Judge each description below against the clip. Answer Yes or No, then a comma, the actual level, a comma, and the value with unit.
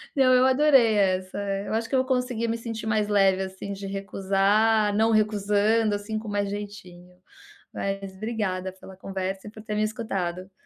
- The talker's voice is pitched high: Yes, high, 205 Hz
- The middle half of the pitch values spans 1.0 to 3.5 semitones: Yes, narrow, 2.4 semitones